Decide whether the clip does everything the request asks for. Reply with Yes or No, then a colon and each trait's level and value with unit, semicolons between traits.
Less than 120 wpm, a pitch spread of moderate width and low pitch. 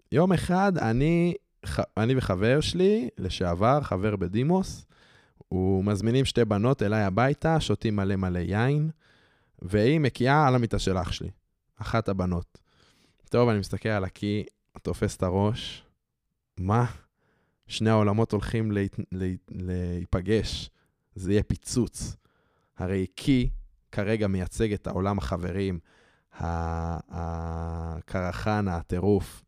Yes: average, 110 wpm; average, 4.4 semitones; low, 105 Hz